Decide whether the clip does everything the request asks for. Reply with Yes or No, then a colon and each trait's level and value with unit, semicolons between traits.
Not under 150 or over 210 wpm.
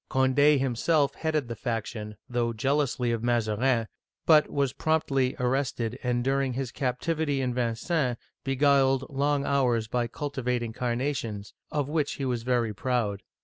No: average, 140 wpm